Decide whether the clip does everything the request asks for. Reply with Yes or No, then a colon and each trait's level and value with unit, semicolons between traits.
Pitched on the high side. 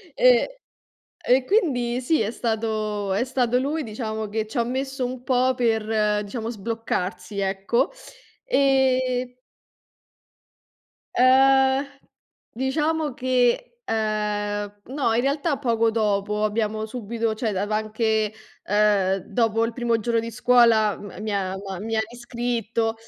Yes: high, 230 Hz